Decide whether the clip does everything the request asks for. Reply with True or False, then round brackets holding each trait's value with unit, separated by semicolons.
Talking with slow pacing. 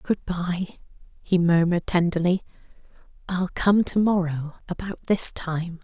True (125 wpm)